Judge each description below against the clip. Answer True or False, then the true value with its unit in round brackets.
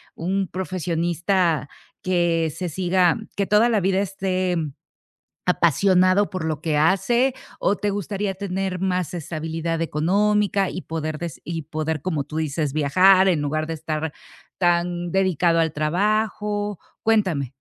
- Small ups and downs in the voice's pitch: False (3.2 semitones)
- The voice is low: False (180 Hz)